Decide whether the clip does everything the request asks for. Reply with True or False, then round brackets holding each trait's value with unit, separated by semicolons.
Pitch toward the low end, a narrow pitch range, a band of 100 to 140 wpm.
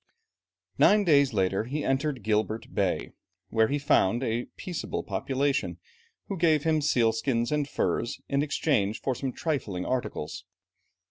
False (130 Hz; 4.8 semitones; 135 wpm)